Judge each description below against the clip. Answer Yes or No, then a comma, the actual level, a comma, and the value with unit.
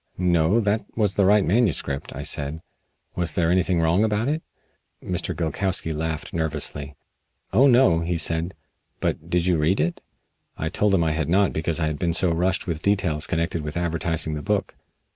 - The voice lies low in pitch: Yes, very low, 85 Hz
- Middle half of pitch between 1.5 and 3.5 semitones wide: Yes, average, 3.0 semitones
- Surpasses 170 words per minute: Yes, average, 180 wpm